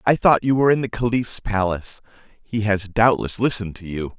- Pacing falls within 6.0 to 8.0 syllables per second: No, 5.7 syllables/s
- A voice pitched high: No, low, 110 Hz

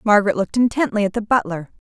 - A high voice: Yes, high, 215 Hz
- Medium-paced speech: Yes, average, 190 wpm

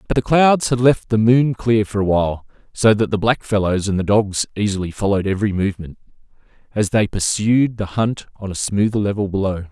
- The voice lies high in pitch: No, low, 105 Hz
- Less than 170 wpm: No, average, 200 wpm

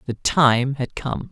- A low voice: Yes, low, 125 Hz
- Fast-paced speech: No, average, 185 wpm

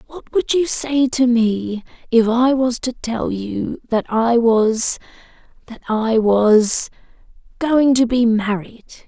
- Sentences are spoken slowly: Yes, slow, 130 wpm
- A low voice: No, high, 235 Hz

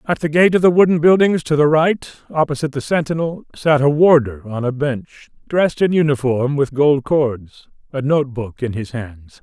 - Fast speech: No, average, 190 wpm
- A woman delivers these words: No, male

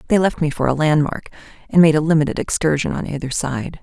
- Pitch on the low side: No, medium, 155 Hz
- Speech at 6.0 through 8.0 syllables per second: Yes, 6.4 syllables/s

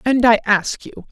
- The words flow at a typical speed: No, fast, 215 wpm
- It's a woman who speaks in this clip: Yes, female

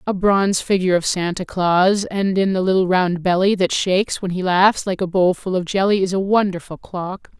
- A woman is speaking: Yes, female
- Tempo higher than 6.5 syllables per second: No, 5.2 syllables/s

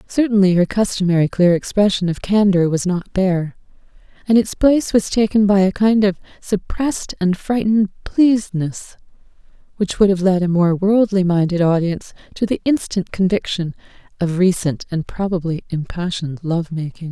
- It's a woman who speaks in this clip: Yes, female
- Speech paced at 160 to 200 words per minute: No, average, 145 wpm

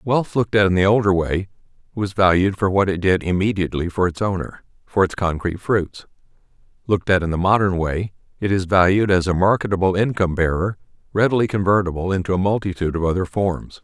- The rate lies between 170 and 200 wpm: Yes, average, 185 wpm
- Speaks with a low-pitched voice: Yes, very low, 95 Hz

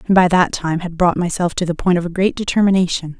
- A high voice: No, medium, 175 Hz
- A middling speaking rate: No, fast, 265 wpm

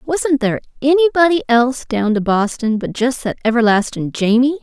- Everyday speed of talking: Yes, average, 155 wpm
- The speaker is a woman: Yes, female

